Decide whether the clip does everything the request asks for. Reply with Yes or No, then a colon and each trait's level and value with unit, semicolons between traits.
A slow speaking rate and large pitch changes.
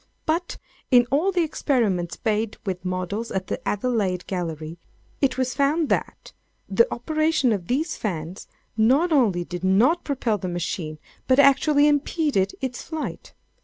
No: average, 145 wpm; wide, 7.7 semitones